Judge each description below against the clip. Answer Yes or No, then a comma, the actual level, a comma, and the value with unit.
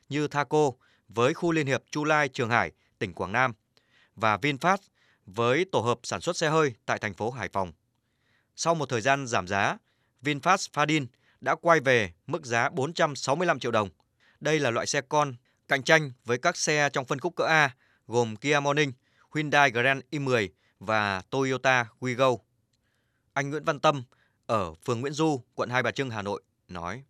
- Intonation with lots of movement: No, average, 4.3 semitones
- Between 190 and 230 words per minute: No, average, 180 wpm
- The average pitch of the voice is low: Yes, low, 130 Hz